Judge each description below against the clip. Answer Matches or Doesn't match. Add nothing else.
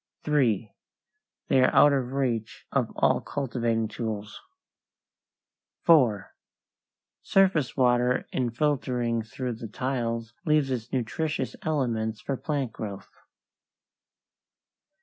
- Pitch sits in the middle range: Doesn't match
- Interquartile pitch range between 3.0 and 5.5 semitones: Matches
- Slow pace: Matches